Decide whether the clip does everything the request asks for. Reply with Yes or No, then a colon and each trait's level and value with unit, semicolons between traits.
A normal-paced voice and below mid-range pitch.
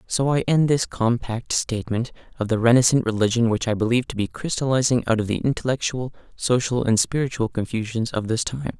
Yes: average, 185 wpm; low, 120 Hz